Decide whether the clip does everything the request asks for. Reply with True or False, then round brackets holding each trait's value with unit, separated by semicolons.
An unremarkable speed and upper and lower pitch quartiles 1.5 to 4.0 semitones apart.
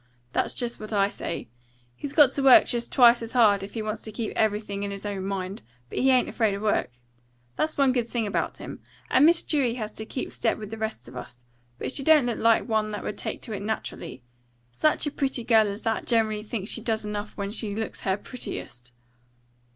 False (230 wpm; 3.1 semitones)